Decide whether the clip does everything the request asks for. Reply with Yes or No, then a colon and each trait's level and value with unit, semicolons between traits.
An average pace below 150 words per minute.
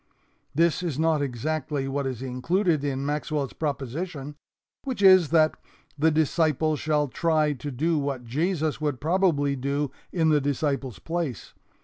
Yes: average, 140 wpm